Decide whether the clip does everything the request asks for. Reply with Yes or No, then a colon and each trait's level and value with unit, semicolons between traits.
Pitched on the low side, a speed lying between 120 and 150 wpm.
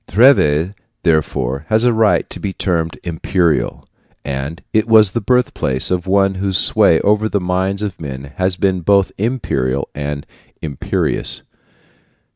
Yes: very low, 95 Hz; average, 140 wpm